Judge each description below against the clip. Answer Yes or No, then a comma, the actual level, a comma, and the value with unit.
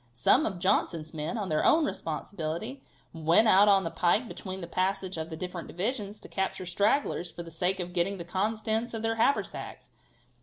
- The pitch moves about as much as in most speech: Yes, average, 4.1 semitones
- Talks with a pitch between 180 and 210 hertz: Yes, high, 190 Hz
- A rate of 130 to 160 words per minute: No, average, 190 wpm